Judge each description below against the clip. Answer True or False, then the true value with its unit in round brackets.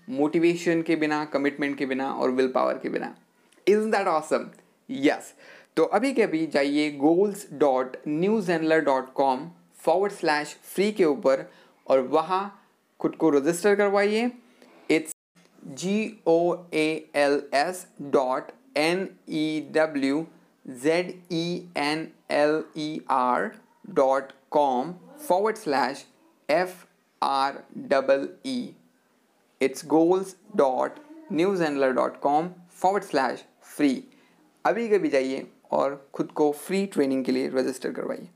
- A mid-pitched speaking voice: True (160 Hz)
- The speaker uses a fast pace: False (130 wpm)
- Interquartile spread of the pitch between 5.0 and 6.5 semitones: True (5.4 semitones)